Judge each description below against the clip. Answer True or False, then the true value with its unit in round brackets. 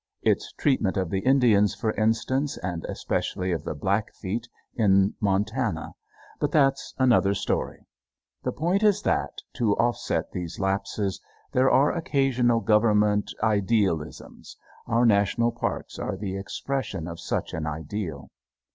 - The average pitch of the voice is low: True (105 Hz)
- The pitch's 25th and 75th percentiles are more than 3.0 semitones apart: True (4.5 semitones)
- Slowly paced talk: True (130 wpm)